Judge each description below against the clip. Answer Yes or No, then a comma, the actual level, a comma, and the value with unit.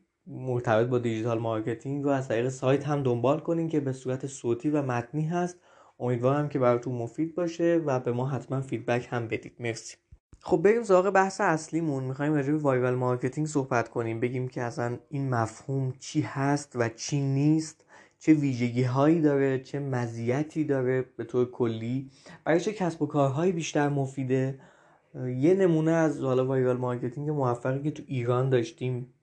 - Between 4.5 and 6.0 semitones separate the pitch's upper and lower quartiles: No, average, 3.5 semitones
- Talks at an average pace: No, fast, 165 wpm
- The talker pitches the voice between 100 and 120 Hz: No, low, 135 Hz